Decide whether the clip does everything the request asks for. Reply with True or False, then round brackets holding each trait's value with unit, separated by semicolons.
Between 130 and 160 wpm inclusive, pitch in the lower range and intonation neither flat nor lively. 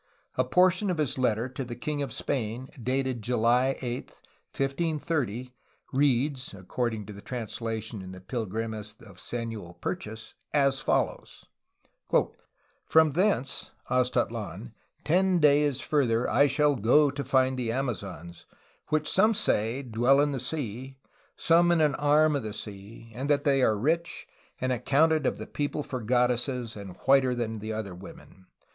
True (150 wpm; 130 Hz; 4.4 semitones)